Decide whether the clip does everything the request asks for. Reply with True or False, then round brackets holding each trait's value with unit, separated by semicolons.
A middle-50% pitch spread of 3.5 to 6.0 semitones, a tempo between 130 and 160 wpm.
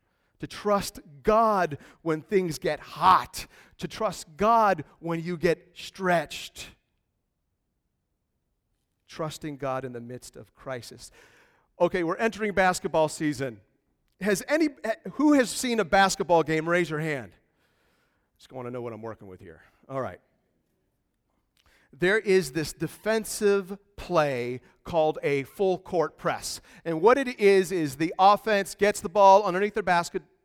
True (5.1 semitones; 140 wpm)